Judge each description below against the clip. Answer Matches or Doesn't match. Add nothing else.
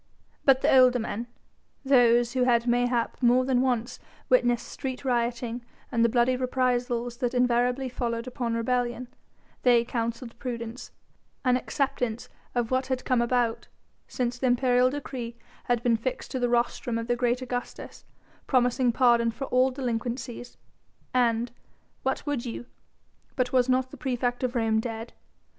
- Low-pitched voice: Doesn't match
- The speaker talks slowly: Doesn't match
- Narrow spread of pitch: Matches